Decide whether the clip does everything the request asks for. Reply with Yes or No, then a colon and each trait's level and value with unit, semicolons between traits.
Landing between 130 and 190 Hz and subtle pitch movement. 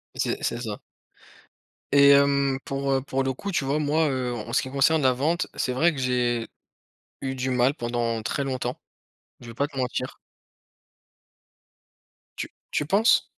Yes: low, 135 Hz; narrow, 2.1 semitones